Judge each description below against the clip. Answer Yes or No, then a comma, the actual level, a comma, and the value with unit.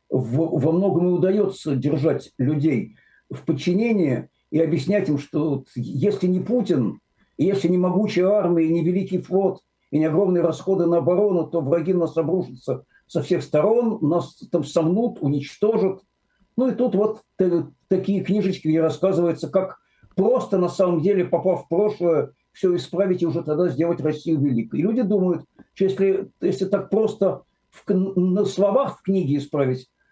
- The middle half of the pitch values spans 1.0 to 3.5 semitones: Yes, average, 3.2 semitones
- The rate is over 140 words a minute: Yes, average, 155 wpm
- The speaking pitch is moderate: Yes, medium, 180 Hz